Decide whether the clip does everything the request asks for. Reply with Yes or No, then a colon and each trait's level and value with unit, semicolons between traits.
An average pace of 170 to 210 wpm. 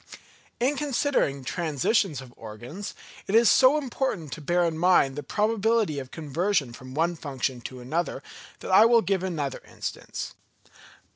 No: average, 150 wpm